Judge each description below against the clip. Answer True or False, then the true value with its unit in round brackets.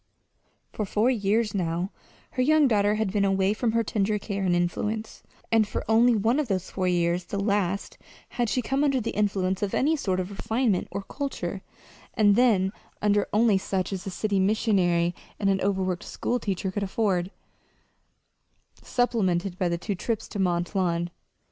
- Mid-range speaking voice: False (200 Hz)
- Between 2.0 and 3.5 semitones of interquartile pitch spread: True (3.1 semitones)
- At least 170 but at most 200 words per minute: True (175 wpm)